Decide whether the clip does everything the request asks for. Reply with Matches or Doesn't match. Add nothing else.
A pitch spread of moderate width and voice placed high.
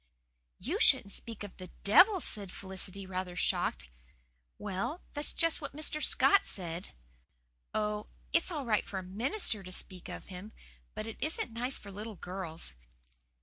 Matches